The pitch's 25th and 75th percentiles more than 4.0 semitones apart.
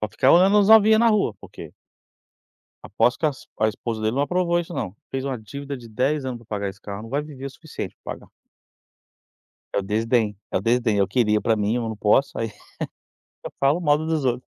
Yes: wide, 5.6 semitones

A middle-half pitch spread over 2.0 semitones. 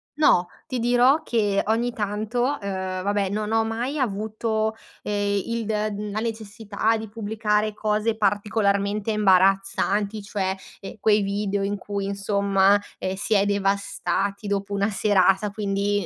No: narrow, 1.7 semitones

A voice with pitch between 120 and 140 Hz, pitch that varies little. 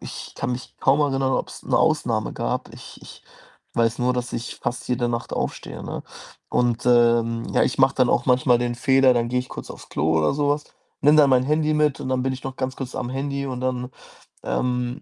Yes: low, 125 Hz; narrow, 1.8 semitones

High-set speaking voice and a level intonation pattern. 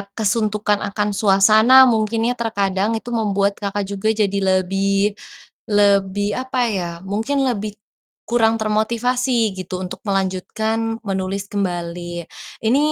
Yes: high, 205 Hz; narrow, 2.3 semitones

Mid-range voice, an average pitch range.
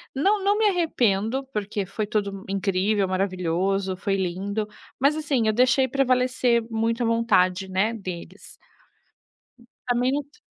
No: high, 215 Hz; average, 4.8 semitones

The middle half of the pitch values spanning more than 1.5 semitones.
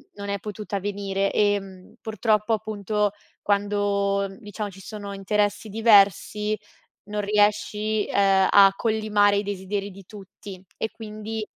No: narrow, 1.1 semitones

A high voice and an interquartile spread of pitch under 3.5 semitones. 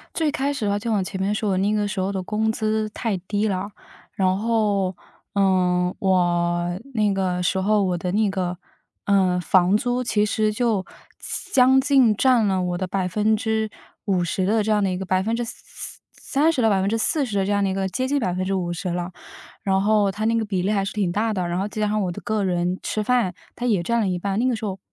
Yes: high, 200 Hz; average, 2.8 semitones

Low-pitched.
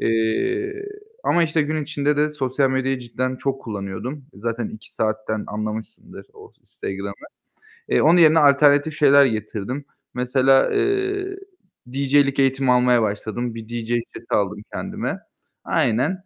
Yes: low, 130 Hz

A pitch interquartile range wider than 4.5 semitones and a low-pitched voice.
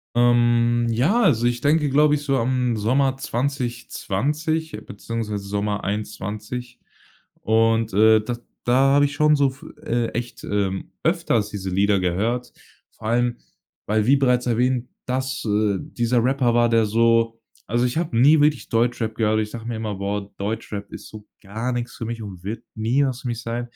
No: average, 2.9 semitones; low, 120 Hz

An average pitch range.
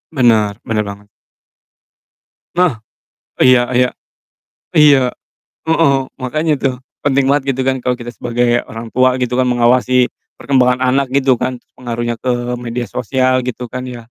No: narrow, 1.7 semitones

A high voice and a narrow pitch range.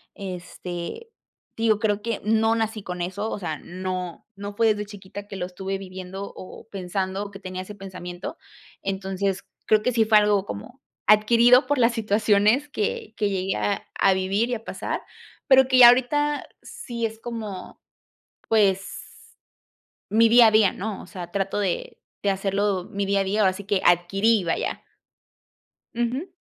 No: high, 205 Hz; average, 3.0 semitones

